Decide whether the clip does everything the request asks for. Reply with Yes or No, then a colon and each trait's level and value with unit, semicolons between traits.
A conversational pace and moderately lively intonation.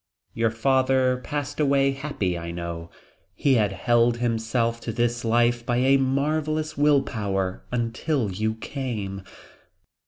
No: slow, 130 wpm; average, 3.8 semitones